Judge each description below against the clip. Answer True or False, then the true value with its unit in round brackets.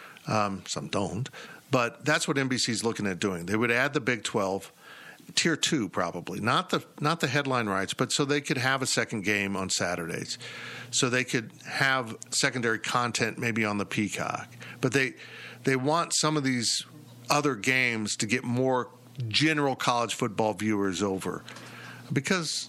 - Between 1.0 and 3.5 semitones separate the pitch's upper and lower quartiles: False (4.4 semitones)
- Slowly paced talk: False (170 wpm)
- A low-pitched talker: True (125 Hz)